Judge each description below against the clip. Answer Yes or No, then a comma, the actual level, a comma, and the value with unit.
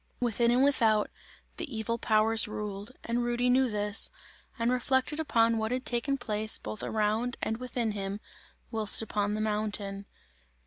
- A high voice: Yes, high, 225 Hz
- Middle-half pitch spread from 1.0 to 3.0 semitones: Yes, narrow, 2.5 semitones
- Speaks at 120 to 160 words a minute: Yes, average, 150 wpm